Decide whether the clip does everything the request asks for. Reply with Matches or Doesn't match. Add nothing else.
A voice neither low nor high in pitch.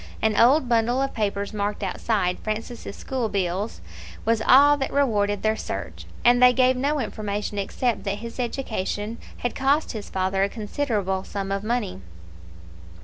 Doesn't match